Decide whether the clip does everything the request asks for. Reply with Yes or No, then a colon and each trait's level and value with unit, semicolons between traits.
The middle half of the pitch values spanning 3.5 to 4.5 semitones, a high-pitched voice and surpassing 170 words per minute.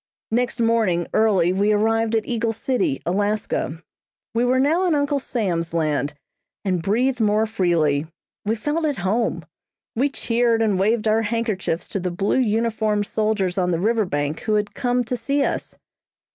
No: average, 4.0 semitones; high, 220 Hz; average, 165 wpm